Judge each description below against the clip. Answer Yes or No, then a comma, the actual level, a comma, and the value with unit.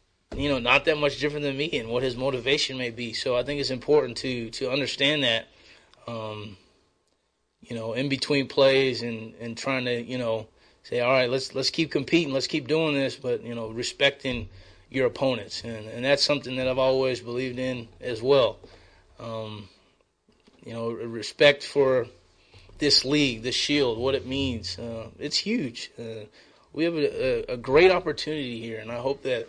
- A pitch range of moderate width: Yes, average, 3.6 semitones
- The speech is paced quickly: No, average, 185 wpm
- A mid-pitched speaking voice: No, low, 130 Hz